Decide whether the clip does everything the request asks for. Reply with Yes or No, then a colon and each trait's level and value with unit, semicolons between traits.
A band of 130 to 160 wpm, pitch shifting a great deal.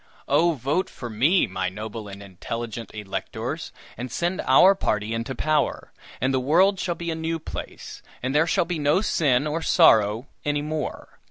No: average, 175 wpm; wide, 6.5 semitones